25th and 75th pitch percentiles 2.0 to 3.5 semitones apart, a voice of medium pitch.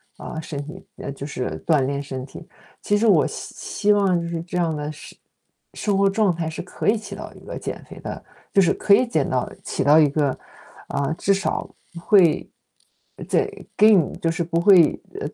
No: average, 4.8 semitones; medium, 170 Hz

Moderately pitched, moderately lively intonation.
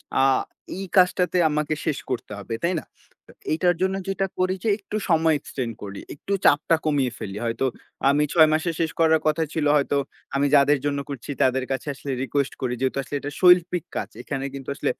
Yes: medium, 145 Hz; average, 4.0 semitones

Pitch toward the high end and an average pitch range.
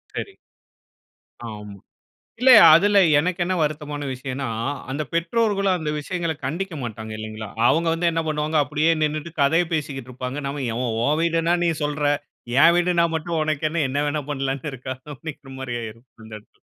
No: medium, 150 Hz; average, 4.0 semitones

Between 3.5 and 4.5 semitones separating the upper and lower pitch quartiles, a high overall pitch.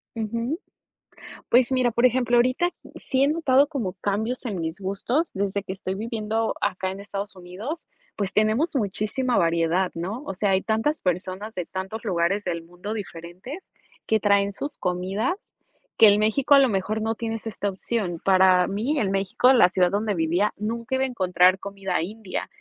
Yes: average, 4.1 semitones; high, 205 Hz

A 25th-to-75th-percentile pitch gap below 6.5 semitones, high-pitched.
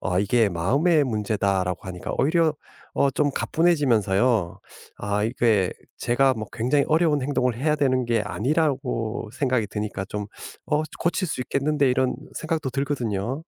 No: wide, 5.6 semitones; low, 125 Hz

